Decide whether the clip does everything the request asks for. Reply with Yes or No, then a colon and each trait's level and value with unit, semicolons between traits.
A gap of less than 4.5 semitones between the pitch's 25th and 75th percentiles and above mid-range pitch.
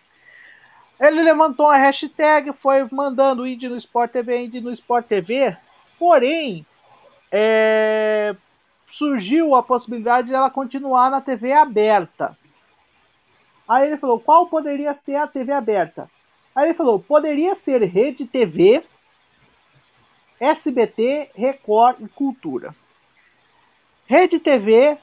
Yes: average, 4.0 semitones; very high, 270 Hz